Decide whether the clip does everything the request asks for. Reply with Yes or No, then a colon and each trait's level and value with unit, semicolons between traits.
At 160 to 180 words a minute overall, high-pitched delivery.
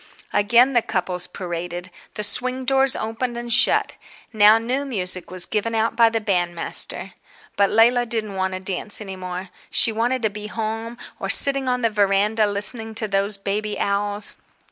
Yes: average, 170 wpm; high, 215 Hz